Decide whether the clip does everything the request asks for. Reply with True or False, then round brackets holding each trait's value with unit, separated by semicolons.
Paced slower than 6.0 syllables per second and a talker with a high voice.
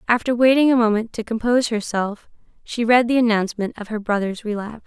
False (6.2 syllables/s; 225 Hz)